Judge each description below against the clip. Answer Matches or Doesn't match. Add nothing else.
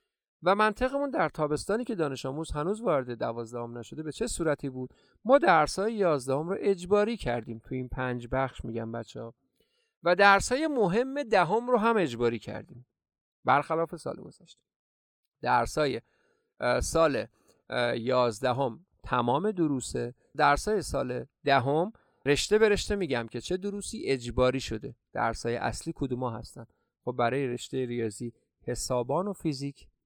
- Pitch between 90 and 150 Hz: Matches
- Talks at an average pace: Matches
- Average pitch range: Doesn't match